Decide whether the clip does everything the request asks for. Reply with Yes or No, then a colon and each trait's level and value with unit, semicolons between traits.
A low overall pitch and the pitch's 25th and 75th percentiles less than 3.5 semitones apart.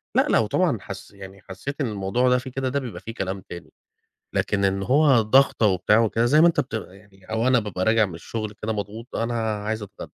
No: low, 110 Hz; average, 4.2 semitones